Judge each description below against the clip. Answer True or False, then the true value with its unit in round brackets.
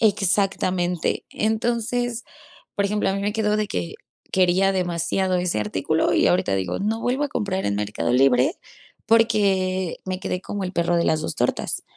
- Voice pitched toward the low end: False (190 Hz)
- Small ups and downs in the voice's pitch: False (3.8 semitones)